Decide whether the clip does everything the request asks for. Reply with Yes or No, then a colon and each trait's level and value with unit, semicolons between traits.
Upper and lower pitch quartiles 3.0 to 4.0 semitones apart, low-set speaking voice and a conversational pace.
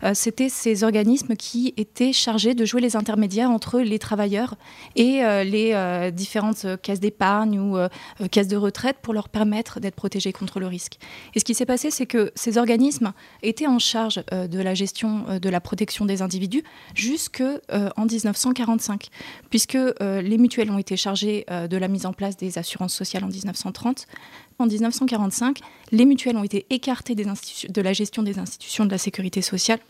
No: average, 3.4 semitones; high, 215 Hz; average, 195 wpm